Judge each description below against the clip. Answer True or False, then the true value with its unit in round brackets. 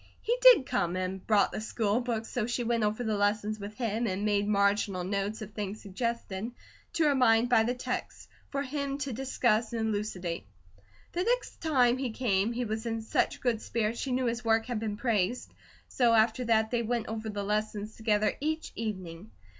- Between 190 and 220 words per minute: True (195 wpm)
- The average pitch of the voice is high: True (220 Hz)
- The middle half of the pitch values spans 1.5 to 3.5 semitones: True (2.8 semitones)